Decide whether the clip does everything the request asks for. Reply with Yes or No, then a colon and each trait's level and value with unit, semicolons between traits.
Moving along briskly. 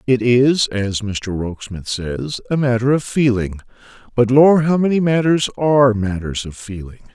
No: average, 160 wpm